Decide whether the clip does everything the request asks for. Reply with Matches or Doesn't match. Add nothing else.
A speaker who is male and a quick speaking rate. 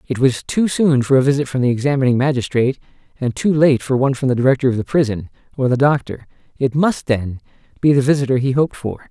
Matches